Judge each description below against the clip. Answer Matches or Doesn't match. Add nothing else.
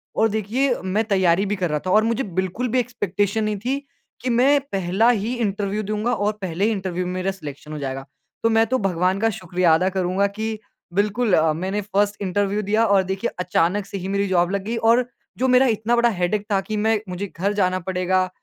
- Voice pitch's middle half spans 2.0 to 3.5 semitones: Matches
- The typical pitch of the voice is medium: Doesn't match